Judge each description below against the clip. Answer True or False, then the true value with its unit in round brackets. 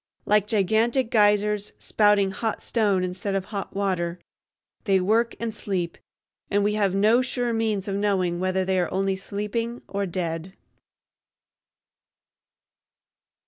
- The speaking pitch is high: True (200 Hz)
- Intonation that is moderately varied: False (2.2 semitones)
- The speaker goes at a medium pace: False (130 wpm)